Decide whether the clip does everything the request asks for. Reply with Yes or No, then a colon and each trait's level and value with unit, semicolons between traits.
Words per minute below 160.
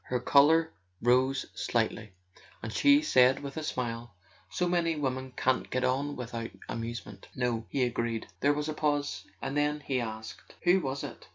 No: average, 175 wpm